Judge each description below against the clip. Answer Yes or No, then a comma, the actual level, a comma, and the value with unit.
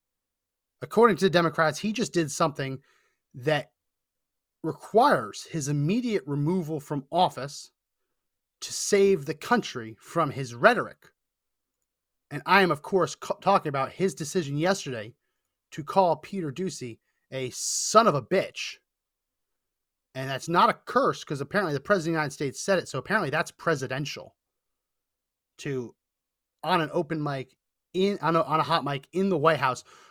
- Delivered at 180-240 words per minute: No, average, 155 wpm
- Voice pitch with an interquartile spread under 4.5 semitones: No, average, 5.2 semitones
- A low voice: No, medium, 160 Hz